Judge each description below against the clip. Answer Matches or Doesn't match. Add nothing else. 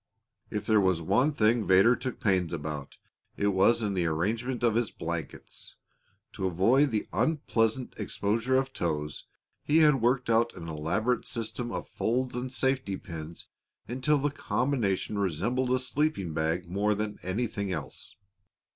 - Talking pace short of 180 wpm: Matches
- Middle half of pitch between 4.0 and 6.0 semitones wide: Matches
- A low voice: Matches